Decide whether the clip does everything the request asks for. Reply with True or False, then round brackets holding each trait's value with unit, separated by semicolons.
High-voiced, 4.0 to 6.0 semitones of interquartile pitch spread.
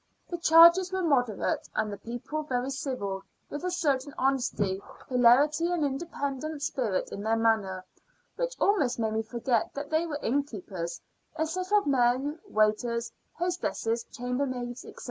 True (265 Hz; 5.3 semitones)